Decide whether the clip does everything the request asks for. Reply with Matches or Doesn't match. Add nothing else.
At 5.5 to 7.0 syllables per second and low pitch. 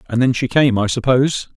Matches